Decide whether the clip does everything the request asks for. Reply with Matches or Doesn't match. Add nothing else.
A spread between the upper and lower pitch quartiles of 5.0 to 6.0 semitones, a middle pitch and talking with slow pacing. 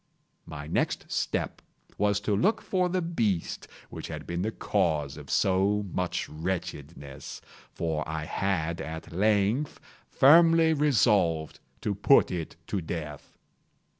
Doesn't match